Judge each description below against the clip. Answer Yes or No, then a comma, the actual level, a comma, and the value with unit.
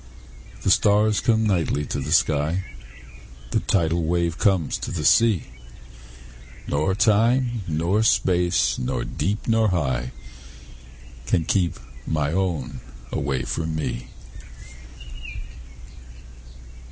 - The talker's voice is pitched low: Yes, very low, 85 Hz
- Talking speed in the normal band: No, slow, 105 wpm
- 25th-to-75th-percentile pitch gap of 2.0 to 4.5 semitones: No, average, 5.2 semitones